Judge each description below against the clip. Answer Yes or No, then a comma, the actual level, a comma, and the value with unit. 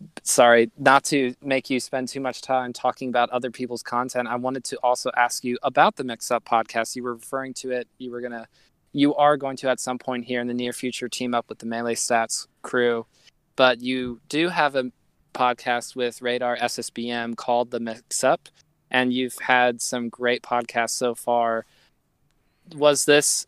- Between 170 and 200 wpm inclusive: Yes, average, 190 wpm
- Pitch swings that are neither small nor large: No, narrow, 1.4 semitones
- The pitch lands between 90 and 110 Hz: No, low, 125 Hz